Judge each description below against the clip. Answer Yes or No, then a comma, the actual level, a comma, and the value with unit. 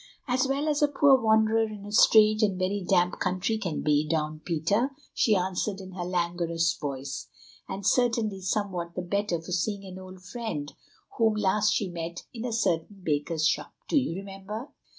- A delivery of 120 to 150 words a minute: No, average, 180 wpm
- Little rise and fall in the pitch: No, average, 4.1 semitones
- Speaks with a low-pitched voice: No, high, 195 Hz